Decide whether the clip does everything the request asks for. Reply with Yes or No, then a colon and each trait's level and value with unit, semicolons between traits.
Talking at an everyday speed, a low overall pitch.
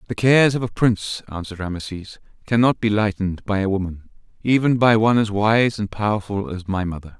Yes: average, 190 wpm; low, 105 Hz